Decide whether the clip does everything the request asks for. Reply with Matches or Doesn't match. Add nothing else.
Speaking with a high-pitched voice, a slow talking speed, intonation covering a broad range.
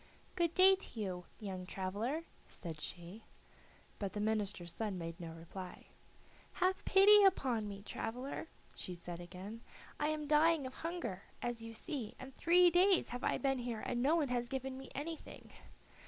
Doesn't match